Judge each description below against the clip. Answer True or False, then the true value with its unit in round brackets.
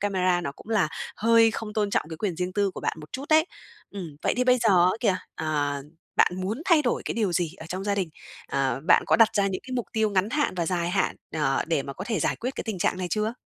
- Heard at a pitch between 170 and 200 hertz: True (195 Hz)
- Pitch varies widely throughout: False (4.6 semitones)